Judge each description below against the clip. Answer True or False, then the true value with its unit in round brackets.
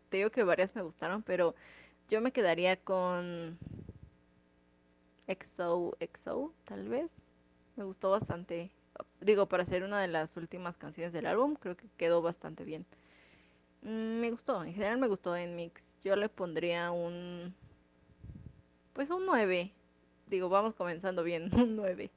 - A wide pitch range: False (4.3 semitones)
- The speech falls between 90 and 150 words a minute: True (145 wpm)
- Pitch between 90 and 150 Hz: False (175 Hz)